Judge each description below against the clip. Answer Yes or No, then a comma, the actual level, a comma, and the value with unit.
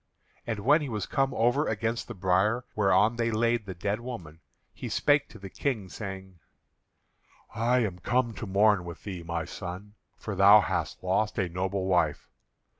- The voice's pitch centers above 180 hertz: No, low, 105 Hz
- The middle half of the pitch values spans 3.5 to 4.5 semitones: Yes, average, 3.8 semitones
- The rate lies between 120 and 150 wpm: No, average, 175 wpm